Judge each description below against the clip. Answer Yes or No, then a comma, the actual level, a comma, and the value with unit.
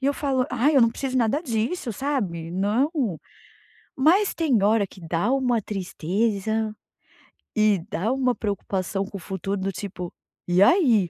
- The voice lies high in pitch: Yes, high, 220 Hz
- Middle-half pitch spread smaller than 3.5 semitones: No, average, 5.0 semitones